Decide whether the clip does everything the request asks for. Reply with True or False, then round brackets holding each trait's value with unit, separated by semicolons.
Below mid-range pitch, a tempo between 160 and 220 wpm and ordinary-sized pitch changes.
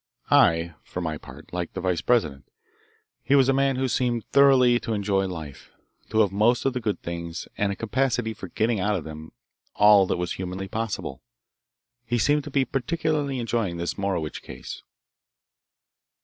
False (105 Hz; 175 wpm; 5.8 semitones)